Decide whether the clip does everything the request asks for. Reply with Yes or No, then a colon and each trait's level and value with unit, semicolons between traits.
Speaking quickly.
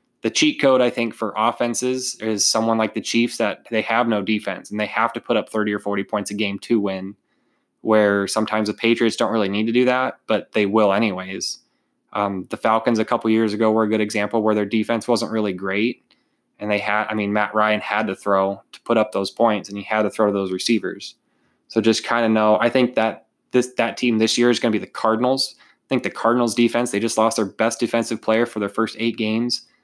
Yes: fast, 240 wpm